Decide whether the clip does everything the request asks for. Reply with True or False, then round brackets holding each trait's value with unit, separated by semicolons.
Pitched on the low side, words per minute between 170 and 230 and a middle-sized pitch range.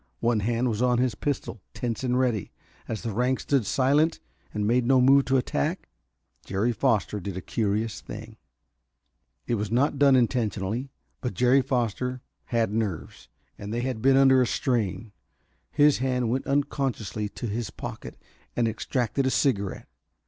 False (120 Hz; 160 wpm; 3.3 semitones)